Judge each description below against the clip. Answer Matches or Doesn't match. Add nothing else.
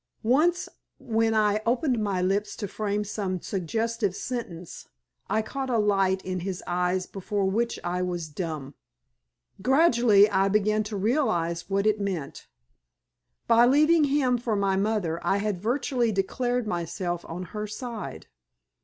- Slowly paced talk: Doesn't match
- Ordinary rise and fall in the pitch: Matches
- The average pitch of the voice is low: Doesn't match